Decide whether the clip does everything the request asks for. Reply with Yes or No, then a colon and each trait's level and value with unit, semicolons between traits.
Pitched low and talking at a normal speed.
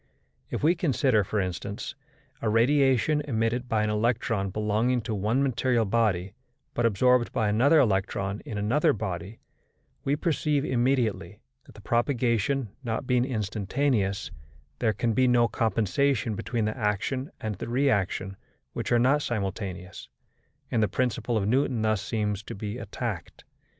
Yes: low, 115 Hz; average, 145 wpm